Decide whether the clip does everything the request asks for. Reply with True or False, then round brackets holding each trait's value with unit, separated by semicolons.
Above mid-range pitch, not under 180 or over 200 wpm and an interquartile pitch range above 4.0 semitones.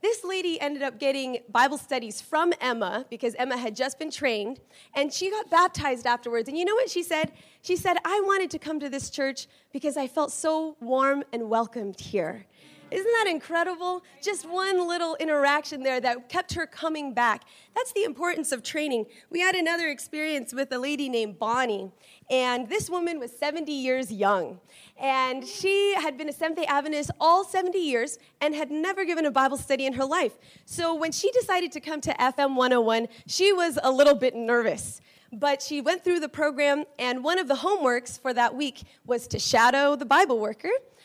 True (295 Hz; 195 wpm; 5.2 semitones)